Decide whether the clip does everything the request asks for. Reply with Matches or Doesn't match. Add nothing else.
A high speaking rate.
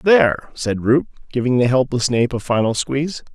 Doesn't match